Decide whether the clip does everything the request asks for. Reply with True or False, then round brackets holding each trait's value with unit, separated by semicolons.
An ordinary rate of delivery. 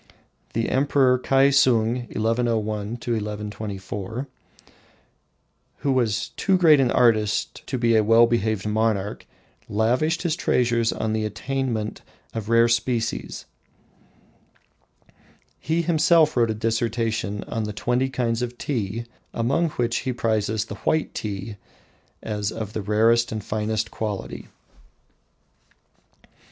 False (115 wpm)